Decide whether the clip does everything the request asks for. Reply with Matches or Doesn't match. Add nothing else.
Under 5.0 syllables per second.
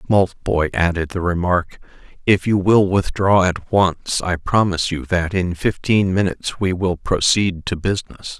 Matches